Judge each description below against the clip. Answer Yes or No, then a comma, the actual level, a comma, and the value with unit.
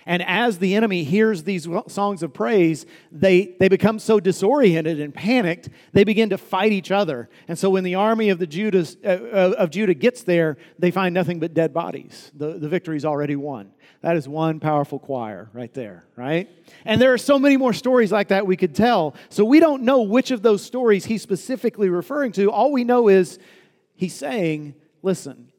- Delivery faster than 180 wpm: Yes, average, 200 wpm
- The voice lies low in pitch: No, high, 190 Hz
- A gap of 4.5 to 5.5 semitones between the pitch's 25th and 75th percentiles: Yes, average, 4.9 semitones